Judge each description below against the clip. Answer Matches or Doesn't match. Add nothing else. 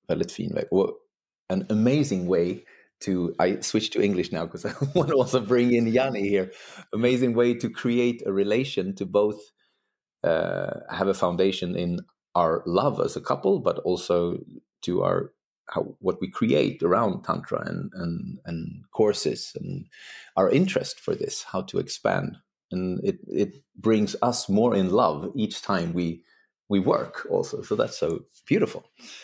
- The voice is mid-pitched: Doesn't match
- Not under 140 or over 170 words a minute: Matches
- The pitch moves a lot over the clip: Matches